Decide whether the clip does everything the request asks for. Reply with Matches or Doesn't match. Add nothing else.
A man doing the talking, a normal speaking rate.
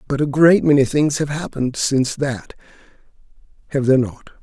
Matches